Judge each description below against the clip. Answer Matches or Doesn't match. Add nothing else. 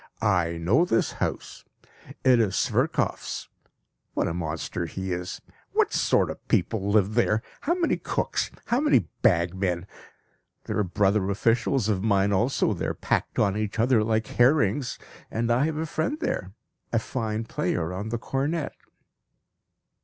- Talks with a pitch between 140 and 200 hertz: Doesn't match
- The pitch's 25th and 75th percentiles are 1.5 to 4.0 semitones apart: Doesn't match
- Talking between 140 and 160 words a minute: Matches